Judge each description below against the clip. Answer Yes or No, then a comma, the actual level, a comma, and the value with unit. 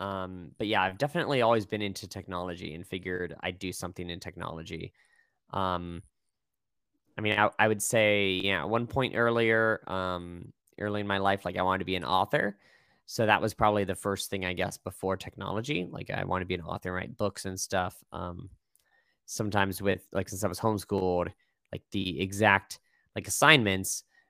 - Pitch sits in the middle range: No, very low, 95 Hz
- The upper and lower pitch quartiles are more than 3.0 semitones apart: No, average, 2.7 semitones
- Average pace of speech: Yes, average, 190 wpm